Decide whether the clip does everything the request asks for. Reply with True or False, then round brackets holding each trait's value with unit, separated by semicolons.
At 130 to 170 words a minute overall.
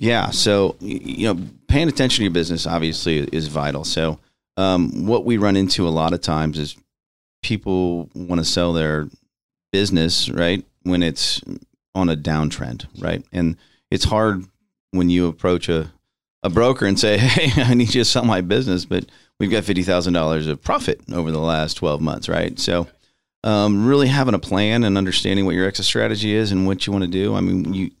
False (190 wpm)